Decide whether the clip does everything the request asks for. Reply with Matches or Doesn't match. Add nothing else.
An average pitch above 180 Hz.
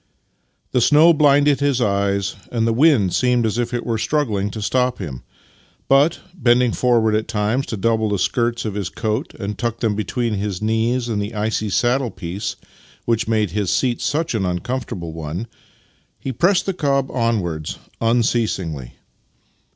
Doesn't match